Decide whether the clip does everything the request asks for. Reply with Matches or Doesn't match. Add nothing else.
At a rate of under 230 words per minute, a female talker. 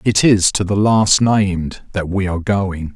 Doesn't match